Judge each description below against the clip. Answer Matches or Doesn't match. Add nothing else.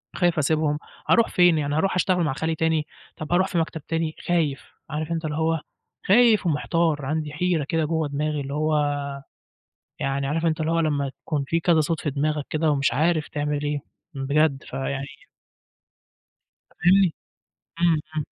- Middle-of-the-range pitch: Matches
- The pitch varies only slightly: Matches